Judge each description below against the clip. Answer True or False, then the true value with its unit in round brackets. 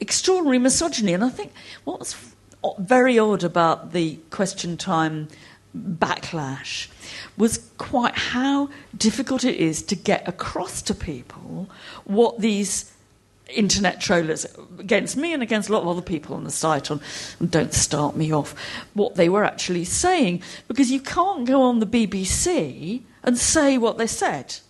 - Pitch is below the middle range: False (200 Hz)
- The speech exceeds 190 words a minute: False (155 wpm)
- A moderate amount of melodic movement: False (7.3 semitones)